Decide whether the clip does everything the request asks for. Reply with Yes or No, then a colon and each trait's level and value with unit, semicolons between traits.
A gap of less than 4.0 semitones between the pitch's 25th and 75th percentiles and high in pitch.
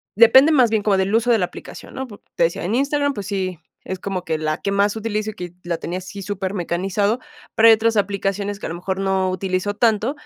Yes: average, 3.1 semitones; high, 200 Hz